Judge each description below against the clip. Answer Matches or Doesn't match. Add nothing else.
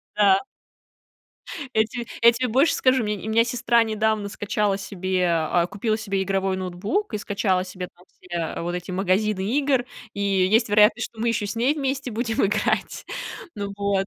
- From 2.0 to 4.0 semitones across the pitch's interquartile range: Matches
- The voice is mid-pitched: Doesn't match